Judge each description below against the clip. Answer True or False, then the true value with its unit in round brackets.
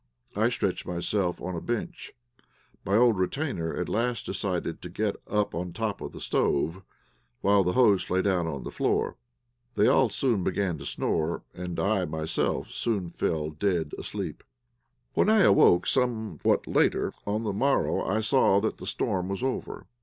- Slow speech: False (170 wpm)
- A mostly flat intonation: False (4.2 semitones)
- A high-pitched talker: False (95 Hz)